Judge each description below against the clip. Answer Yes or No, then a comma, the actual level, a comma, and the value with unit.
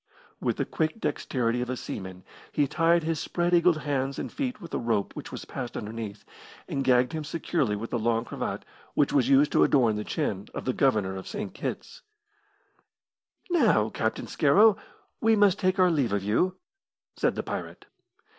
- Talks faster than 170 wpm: Yes, average, 180 wpm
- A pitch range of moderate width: No, wide, 7.1 semitones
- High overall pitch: No, low, 135 Hz